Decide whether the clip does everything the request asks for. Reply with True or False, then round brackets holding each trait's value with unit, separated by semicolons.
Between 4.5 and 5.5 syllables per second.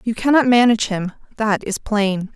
True (5.0 syllables/s)